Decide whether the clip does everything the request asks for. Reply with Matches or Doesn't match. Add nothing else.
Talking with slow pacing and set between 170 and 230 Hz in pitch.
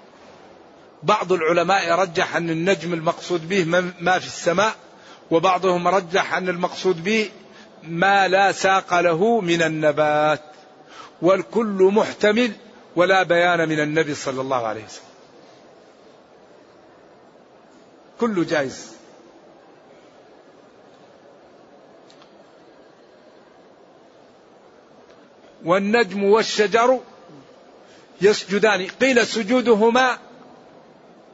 Doesn't match